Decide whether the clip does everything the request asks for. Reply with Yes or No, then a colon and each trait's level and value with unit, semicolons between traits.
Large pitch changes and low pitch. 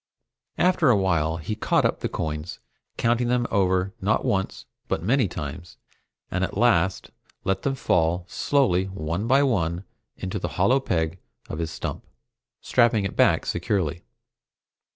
Yes: wide, 5.7 semitones; very low, 95 Hz